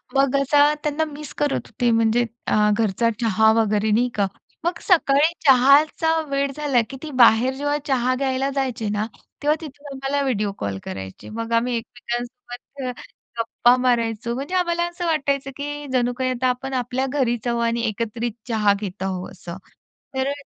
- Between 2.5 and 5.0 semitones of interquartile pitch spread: Yes, average, 3.6 semitones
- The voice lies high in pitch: Yes, very high, 250 Hz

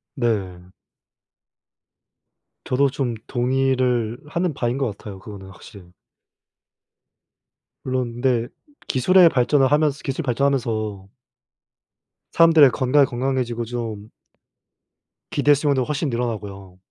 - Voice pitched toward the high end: No, low, 125 Hz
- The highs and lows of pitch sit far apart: No, average, 3.9 semitones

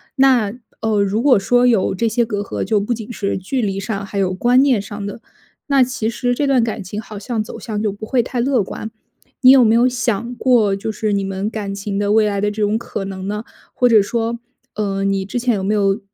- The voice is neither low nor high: No, high, 215 Hz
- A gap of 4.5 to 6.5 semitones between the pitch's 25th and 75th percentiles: No, average, 3.3 semitones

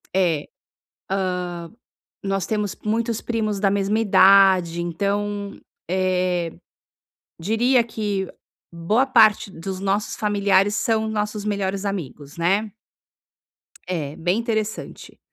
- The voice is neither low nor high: No, high, 200 Hz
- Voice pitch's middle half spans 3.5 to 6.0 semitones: No, narrow, 2.6 semitones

